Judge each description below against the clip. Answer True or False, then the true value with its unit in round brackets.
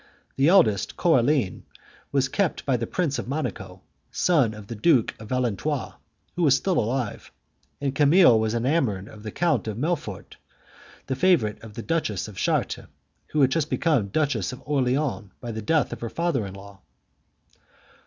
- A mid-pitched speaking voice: False (130 Hz)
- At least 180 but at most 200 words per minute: False (170 wpm)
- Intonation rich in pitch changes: True (6.0 semitones)